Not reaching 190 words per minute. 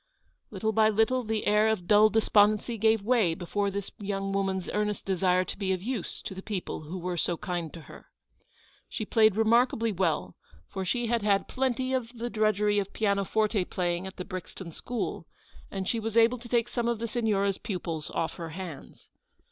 No: average, 195 wpm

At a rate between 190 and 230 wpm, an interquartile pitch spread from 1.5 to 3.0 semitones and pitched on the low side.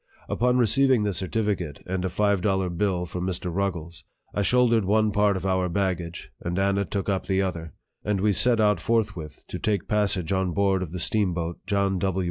Yes: average, 200 wpm; narrow, 2.6 semitones; very low, 95 Hz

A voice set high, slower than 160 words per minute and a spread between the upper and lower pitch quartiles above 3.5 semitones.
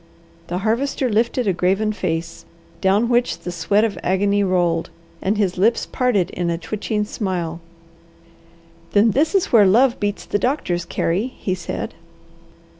Yes: high, 205 Hz; average, 150 wpm; average, 4.1 semitones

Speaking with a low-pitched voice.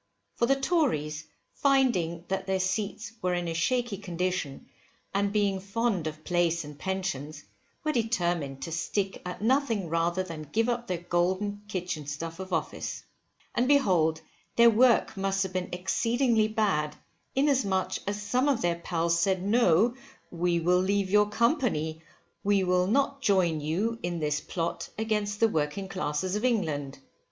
No: high, 190 Hz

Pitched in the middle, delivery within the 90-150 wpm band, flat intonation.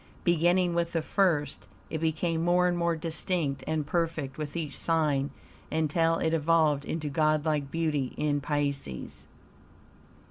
Yes: medium, 160 Hz; slow, 135 wpm; narrow, 2.3 semitones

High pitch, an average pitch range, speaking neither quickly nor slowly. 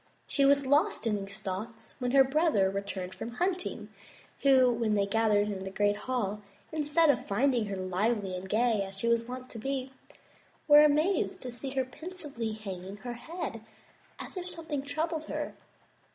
No: high, 240 Hz; wide, 5.7 semitones; average, 170 wpm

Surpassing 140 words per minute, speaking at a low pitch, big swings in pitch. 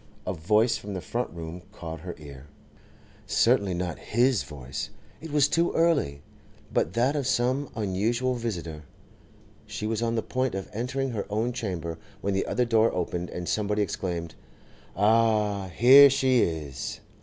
Yes: average, 150 wpm; low, 105 Hz; wide, 5.9 semitones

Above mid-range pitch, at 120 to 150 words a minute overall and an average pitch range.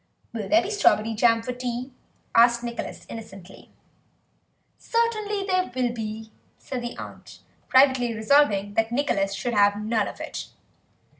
Yes: high, 235 Hz; average, 140 wpm; average, 4.1 semitones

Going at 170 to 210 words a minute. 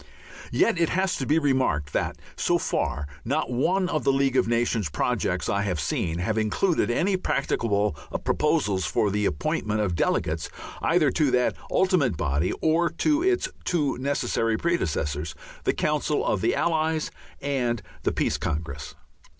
No: average, 155 wpm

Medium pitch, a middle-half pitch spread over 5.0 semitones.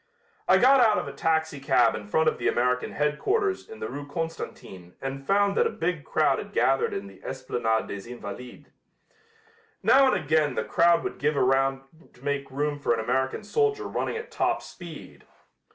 Yes: medium, 145 Hz; wide, 5.4 semitones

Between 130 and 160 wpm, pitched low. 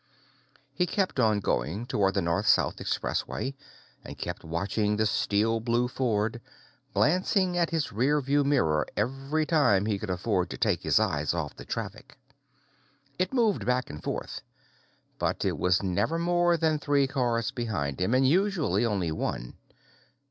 Yes: average, 155 wpm; low, 120 Hz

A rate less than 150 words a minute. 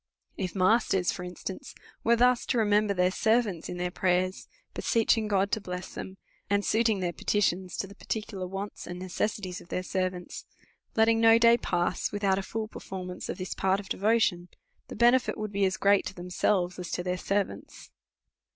No: average, 185 wpm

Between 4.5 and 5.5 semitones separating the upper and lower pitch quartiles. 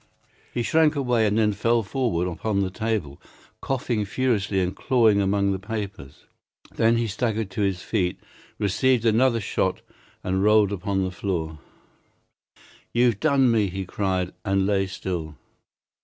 No: average, 3.5 semitones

